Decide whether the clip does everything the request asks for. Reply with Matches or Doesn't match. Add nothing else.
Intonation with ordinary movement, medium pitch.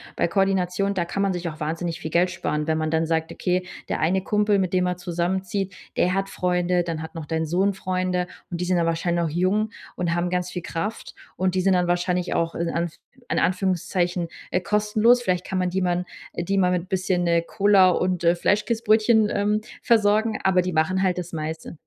Doesn't match